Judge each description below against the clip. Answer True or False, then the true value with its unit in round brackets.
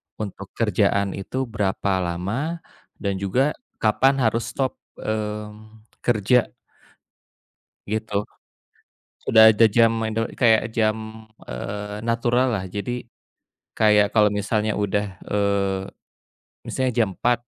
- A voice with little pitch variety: True (2.2 semitones)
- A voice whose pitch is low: True (110 Hz)